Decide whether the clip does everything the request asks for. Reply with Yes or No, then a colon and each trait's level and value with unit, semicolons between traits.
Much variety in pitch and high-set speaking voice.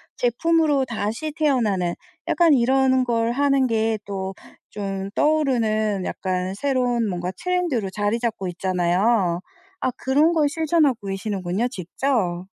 Yes: wide, 6.0 semitones; high, 230 Hz